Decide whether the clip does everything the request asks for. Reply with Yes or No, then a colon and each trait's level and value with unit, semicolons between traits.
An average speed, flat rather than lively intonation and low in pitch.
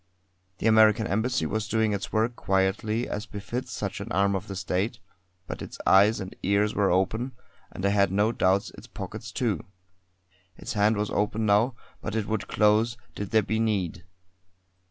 Yes: average, 175 wpm; narrow, 2.0 semitones; low, 105 Hz